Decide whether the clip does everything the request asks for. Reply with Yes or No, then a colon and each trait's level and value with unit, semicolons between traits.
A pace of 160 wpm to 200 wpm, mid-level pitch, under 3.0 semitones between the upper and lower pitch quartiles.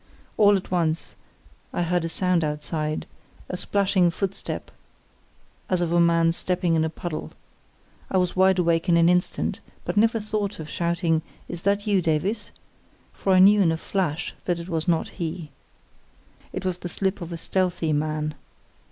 Yes: average, 170 wpm; medium, 175 Hz; narrow, 2.4 semitones